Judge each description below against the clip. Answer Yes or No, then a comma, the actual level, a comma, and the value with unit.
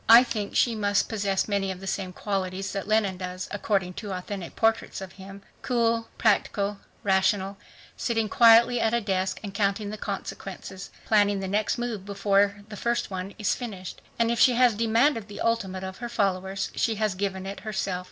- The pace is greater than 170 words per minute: Yes, average, 185 wpm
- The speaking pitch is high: Yes, high, 200 Hz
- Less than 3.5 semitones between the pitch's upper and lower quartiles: Yes, average, 2.7 semitones